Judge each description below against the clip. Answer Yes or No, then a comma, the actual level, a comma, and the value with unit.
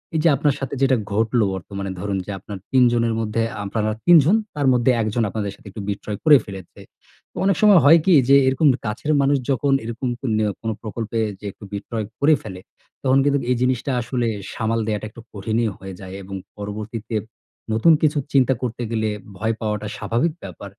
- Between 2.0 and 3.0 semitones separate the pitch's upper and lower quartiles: No, average, 4.2 semitones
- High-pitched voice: No, low, 115 Hz